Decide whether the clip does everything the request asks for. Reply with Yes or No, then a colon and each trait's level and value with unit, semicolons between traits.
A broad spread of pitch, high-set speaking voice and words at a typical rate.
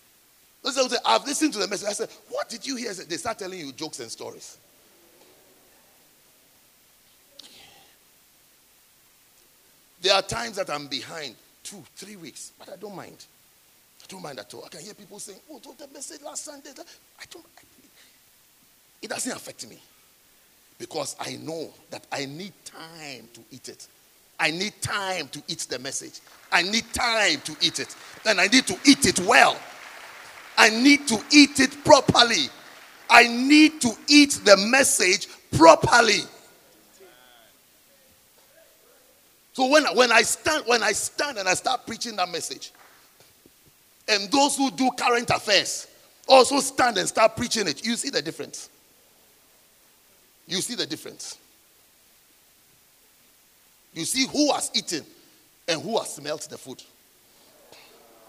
Yes: wide, 6.6 semitones; high, 240 Hz; average, 145 wpm